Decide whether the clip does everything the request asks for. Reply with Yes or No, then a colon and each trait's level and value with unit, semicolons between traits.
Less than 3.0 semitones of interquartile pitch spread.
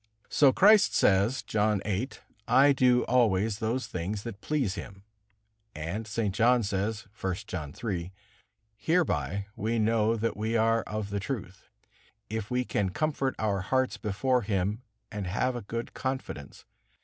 No: average, 3.9 semitones